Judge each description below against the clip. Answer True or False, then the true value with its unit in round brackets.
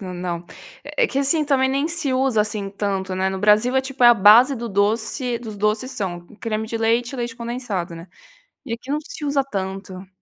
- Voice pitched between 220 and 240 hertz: True (230 Hz)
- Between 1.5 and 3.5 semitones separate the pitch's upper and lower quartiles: False (4.9 semitones)